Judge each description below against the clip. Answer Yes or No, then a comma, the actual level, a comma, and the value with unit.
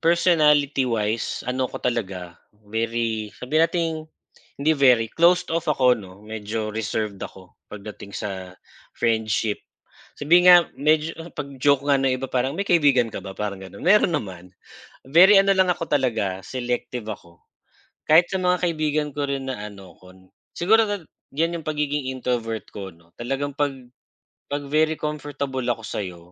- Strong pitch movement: Yes, wide, 6.1 semitones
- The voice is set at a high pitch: No, low, 130 Hz